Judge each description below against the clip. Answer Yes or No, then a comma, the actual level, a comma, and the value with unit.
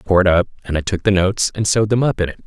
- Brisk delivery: Yes, fast, 365 wpm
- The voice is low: Yes, very low, 95 Hz